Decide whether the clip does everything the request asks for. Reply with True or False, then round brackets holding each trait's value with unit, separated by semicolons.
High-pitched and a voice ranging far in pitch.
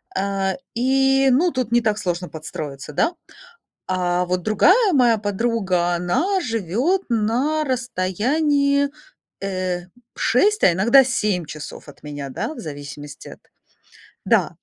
True (210 Hz; 7.2 semitones)